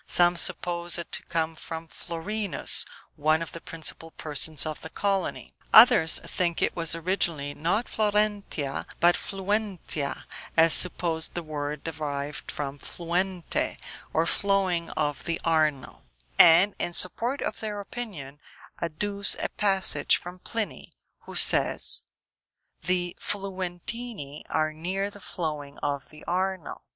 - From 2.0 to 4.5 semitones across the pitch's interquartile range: Yes, average, 3.7 semitones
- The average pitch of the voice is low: No, medium, 170 Hz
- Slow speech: Yes, slow, 130 wpm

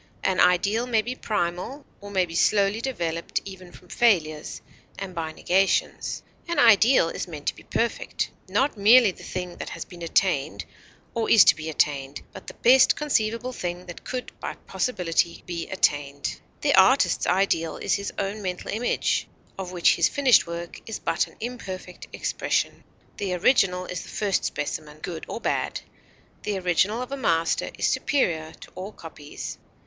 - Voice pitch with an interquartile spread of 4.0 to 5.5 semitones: Yes, average, 4.7 semitones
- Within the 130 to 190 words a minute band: Yes, average, 170 wpm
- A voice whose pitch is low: No, medium, 185 Hz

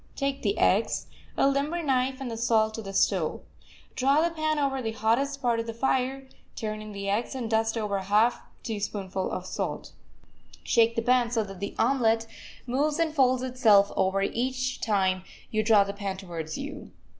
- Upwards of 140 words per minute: Yes, average, 190 wpm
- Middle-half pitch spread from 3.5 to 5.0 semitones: Yes, average, 4.5 semitones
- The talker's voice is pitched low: No, high, 230 Hz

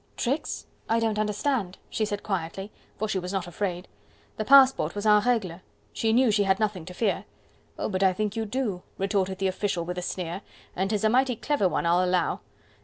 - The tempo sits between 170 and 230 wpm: Yes, fast, 205 wpm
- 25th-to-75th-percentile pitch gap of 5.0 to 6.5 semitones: No, average, 3.1 semitones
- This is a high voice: Yes, high, 200 Hz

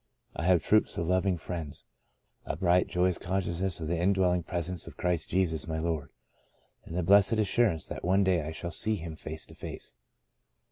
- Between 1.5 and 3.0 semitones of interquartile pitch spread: Yes, narrow, 2.5 semitones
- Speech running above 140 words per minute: Yes, average, 190 wpm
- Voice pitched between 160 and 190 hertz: No, very low, 90 Hz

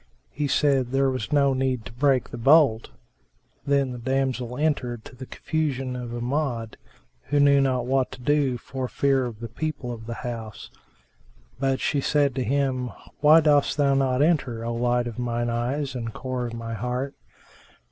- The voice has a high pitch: No, low, 130 Hz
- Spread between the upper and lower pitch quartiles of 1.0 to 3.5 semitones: Yes, narrow, 2.6 semitones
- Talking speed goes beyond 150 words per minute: Yes, average, 180 wpm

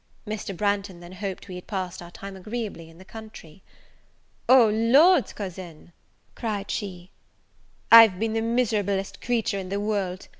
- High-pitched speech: Yes, high, 200 Hz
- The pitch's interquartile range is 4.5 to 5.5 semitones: No, average, 3.3 semitones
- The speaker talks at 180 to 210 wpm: No, average, 150 wpm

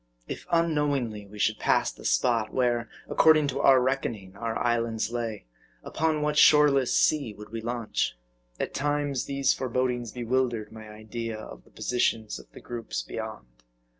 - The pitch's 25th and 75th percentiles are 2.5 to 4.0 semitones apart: Yes, average, 3.7 semitones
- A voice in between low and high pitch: No, low, 120 Hz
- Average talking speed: Yes, average, 155 wpm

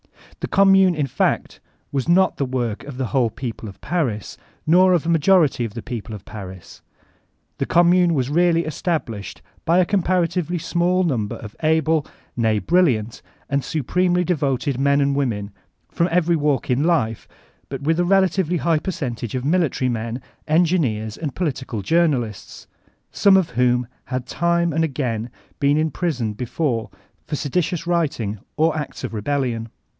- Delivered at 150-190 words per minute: Yes, average, 160 wpm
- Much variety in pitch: Yes, wide, 6.1 semitones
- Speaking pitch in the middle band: Yes, medium, 145 Hz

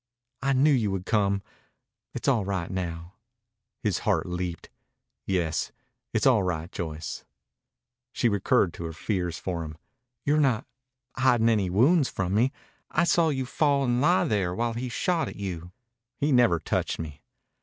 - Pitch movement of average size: No, wide, 6.6 semitones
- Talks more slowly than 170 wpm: Yes, average, 160 wpm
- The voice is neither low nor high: No, low, 100 Hz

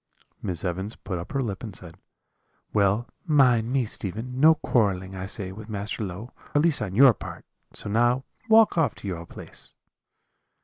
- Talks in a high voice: No, low, 110 Hz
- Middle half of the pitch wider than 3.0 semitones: Yes, average, 5.0 semitones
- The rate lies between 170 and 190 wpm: Yes, average, 175 wpm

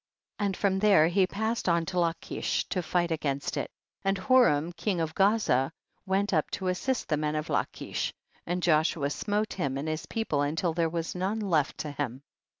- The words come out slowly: No, average, 195 wpm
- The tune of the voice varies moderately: Yes, average, 4.2 semitones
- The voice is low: No, medium, 175 Hz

